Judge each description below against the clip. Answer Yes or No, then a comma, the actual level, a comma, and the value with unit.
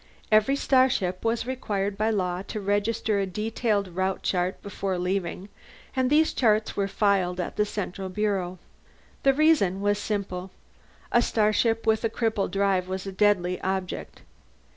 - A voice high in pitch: Yes, high, 200 Hz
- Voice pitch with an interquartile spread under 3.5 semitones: Yes, average, 2.8 semitones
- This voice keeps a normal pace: Yes, average, 150 wpm